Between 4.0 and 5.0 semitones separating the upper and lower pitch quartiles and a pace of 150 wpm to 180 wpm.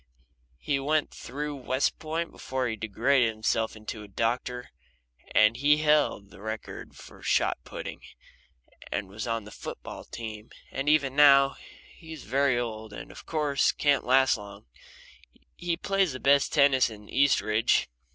Yes: average, 4.6 semitones; average, 160 wpm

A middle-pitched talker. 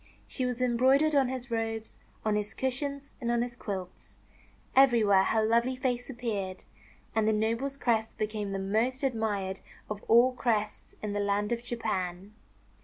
No: high, 230 Hz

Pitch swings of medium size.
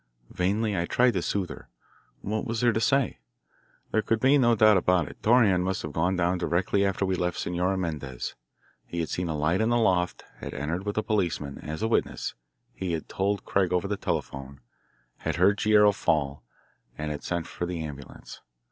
Yes: average, 4.0 semitones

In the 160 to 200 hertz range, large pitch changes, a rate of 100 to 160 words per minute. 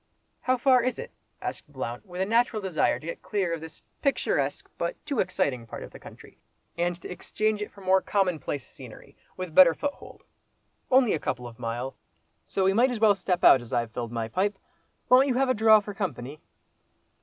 No: high, 190 Hz; wide, 7.2 semitones; average, 200 wpm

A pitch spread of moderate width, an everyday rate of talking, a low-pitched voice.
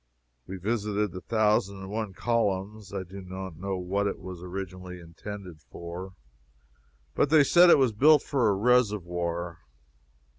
Yes: average, 3.0 semitones; average, 150 wpm; very low, 95 Hz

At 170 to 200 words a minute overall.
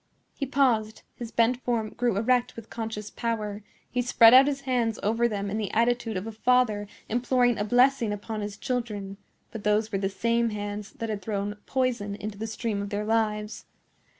Yes: average, 190 wpm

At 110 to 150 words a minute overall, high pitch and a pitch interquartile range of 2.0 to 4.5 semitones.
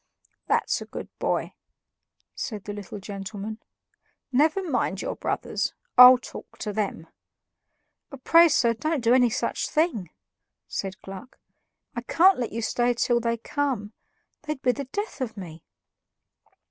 No: average, 140 wpm; high, 240 Hz; average, 5.1 semitones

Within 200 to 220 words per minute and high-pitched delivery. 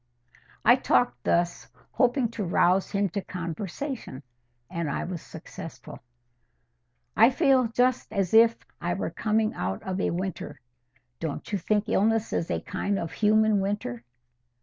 No: average, 145 wpm; high, 200 Hz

